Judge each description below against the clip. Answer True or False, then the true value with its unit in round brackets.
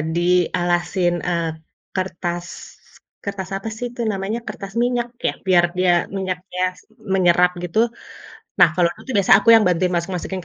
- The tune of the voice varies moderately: False (2.0 semitones)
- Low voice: False (185 Hz)